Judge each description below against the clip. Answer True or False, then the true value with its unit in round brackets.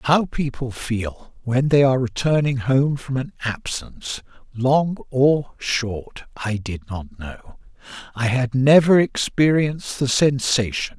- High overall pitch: False (130 Hz)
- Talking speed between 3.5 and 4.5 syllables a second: True (3.7 syllables/s)